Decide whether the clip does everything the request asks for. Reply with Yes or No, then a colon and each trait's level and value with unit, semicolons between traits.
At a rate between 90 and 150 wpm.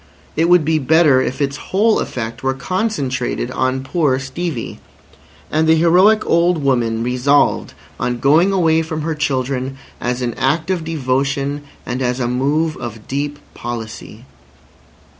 Yes: average, 145 wpm